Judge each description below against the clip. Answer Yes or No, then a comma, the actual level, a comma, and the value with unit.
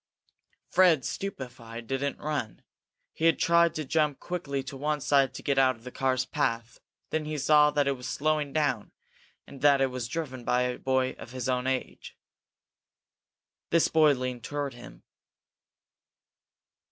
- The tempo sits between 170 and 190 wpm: No, average, 155 wpm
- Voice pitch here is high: No, low, 135 Hz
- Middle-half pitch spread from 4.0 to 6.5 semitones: No, average, 2.9 semitones